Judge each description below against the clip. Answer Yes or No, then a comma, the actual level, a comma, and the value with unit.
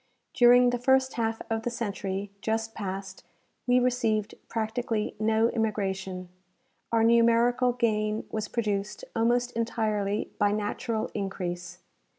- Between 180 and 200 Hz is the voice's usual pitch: No, high, 220 Hz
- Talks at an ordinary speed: No, slow, 120 wpm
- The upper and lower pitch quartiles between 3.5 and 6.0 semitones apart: No, narrow, 2.4 semitones